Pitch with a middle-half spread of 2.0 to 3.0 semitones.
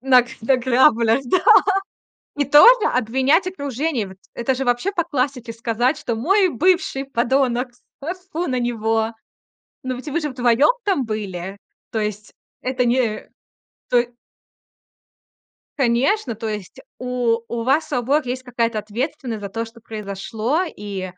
No: average, 3.6 semitones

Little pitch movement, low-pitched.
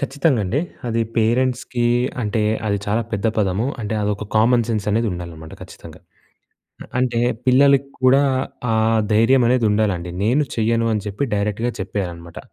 No: average, 3.4 semitones; low, 110 Hz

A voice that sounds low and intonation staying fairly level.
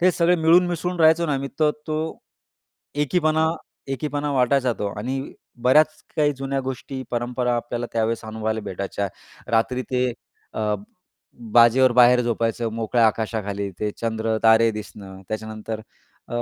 No: low, 120 Hz; average, 4.5 semitones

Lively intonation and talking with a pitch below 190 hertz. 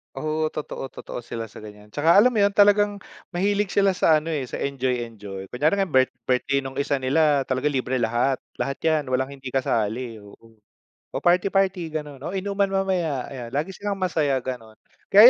Yes: wide, 6.4 semitones; medium, 140 Hz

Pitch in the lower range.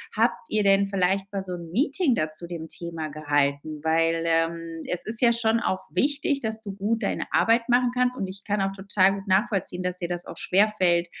No: high, 190 Hz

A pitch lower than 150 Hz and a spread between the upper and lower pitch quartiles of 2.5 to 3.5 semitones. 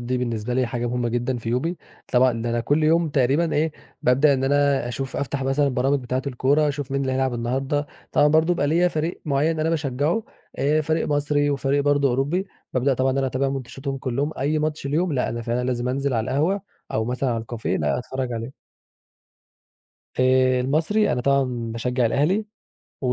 Yes: low, 135 Hz; average, 2.9 semitones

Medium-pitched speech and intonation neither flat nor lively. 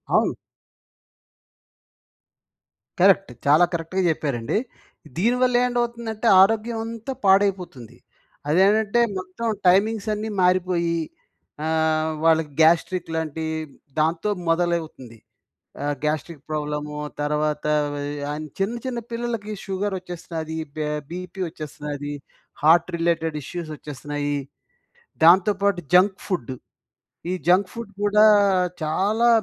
Yes: medium, 175 Hz; average, 4.8 semitones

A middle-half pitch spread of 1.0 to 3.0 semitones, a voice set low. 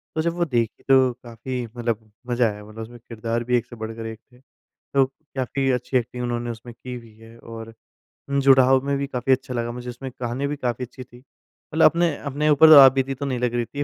Yes: narrow, 2.5 semitones; low, 125 Hz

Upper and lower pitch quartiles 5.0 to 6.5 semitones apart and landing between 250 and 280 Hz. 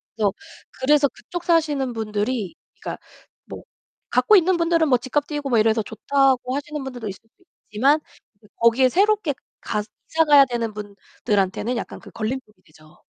Yes: average, 5.3 semitones; very high, 255 Hz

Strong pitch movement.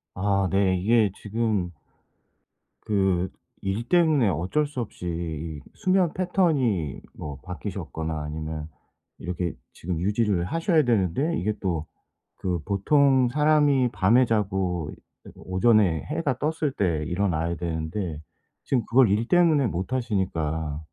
Yes: wide, 6.8 semitones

